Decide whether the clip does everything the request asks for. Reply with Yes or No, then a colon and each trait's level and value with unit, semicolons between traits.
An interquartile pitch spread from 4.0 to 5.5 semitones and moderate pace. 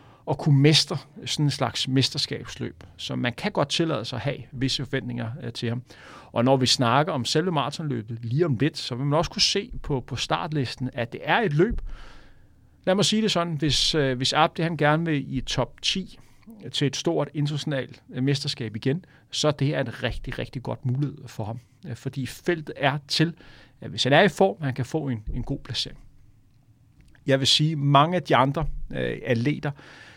No: average, 3.4 semitones; average, 195 wpm